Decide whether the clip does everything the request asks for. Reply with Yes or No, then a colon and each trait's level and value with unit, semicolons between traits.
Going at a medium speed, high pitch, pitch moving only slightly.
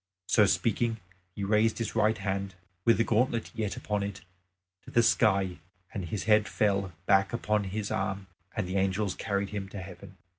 No: average, 180 wpm; low, 100 Hz; narrow, 1.9 semitones